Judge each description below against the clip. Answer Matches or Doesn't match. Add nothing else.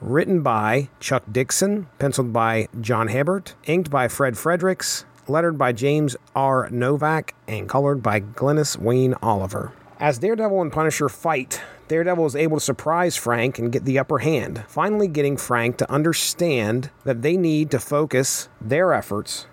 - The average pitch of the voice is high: Doesn't match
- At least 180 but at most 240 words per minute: Doesn't match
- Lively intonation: Doesn't match